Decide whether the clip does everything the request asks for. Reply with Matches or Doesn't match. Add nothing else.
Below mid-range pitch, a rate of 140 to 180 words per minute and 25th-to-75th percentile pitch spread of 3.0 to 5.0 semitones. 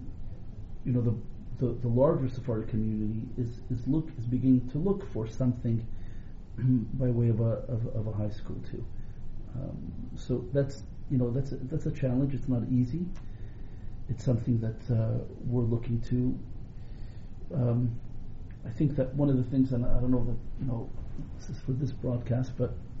Doesn't match